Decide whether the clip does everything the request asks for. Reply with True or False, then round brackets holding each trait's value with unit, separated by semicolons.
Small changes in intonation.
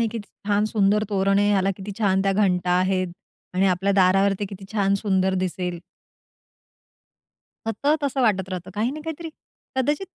True (2.1 semitones)